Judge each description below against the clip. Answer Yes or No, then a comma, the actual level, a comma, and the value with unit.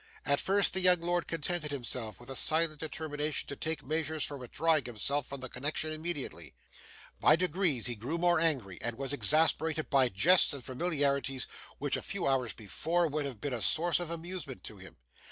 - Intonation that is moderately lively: Yes, average, 4.0 semitones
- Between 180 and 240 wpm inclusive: Yes, average, 190 wpm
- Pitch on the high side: No, medium, 150 Hz